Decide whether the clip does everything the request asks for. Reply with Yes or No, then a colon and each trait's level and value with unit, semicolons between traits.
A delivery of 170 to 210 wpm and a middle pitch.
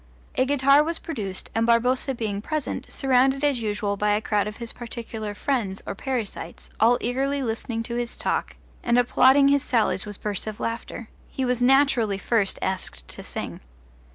No: average, 175 wpm; high, 235 Hz